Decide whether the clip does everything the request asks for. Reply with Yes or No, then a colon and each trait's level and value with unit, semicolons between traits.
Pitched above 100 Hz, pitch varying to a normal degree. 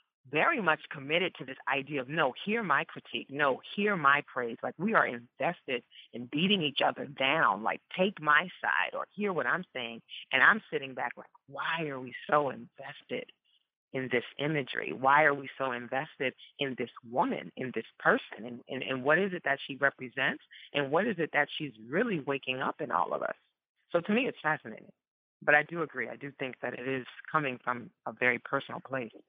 Yes: medium, 140 Hz; average, 3.5 semitones